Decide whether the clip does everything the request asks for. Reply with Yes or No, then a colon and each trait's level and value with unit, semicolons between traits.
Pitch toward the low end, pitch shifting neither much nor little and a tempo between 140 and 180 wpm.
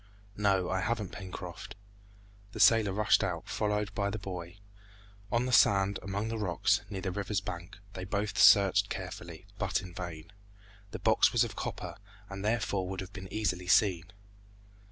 No: low, 100 Hz; narrow, 2.2 semitones; average, 165 wpm